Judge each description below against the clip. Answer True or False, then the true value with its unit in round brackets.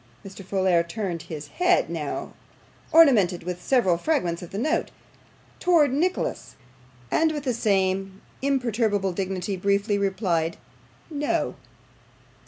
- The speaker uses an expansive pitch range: True (6.8 semitones)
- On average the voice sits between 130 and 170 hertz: False (200 Hz)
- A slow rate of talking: True (115 wpm)